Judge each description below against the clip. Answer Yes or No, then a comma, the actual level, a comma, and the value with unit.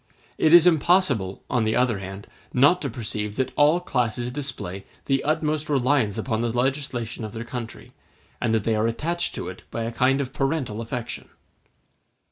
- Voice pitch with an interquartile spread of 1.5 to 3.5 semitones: No, average, 4.4 semitones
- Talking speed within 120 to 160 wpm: No, average, 175 wpm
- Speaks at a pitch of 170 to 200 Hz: No, low, 125 Hz